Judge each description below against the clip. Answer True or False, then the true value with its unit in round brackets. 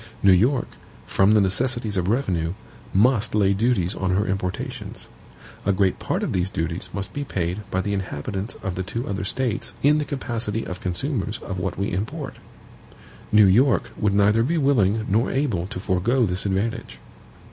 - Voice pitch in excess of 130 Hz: False (100 Hz)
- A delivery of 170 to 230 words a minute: True (175 wpm)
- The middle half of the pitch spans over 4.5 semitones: False (4.0 semitones)